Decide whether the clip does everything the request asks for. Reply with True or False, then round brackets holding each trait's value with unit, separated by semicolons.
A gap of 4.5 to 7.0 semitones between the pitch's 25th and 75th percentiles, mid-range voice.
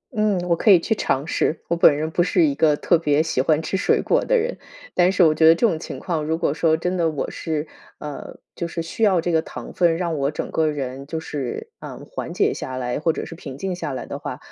False (2.9 semitones; 160 Hz)